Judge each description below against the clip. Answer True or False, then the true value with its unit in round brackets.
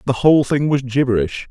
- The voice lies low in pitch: True (130 Hz)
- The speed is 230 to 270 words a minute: False (200 wpm)